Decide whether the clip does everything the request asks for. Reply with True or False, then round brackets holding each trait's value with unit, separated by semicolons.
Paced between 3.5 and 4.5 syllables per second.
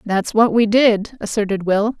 True (4.3 syllables/s)